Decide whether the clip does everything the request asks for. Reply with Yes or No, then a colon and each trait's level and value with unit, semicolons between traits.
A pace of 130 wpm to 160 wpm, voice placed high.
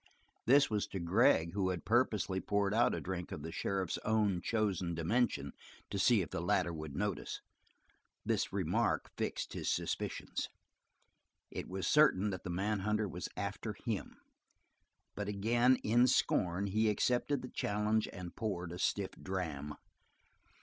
No: average, 150 wpm; low, 100 Hz